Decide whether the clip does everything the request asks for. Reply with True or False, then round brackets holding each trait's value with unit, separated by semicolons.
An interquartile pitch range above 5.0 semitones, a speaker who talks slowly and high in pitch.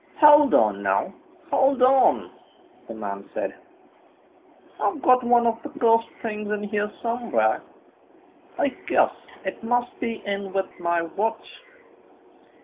False (4.0 semitones; 130 wpm; 225 Hz)